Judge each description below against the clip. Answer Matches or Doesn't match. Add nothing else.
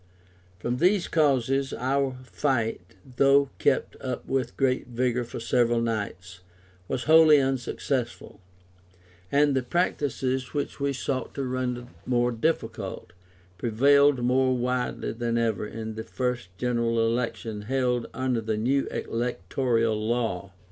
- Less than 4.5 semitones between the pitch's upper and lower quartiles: Matches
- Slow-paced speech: Matches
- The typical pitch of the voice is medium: Doesn't match